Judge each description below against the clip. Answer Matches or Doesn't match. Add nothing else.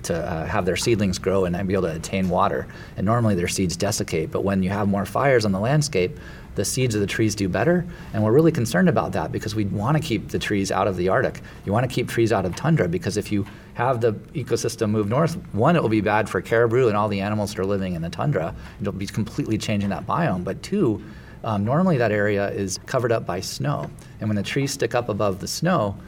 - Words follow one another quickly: Matches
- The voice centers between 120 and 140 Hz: Doesn't match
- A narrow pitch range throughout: Doesn't match